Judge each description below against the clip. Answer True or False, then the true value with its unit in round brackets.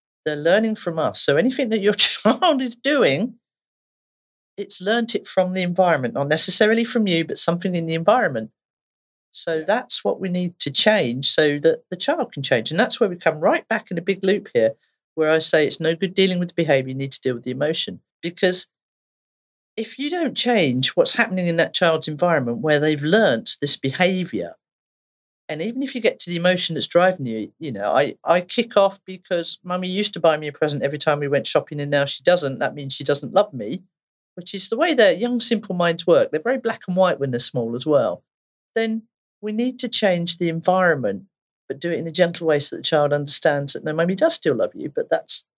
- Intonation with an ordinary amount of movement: False (5.9 semitones)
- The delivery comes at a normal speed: False (225 wpm)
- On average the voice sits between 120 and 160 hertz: False (180 Hz)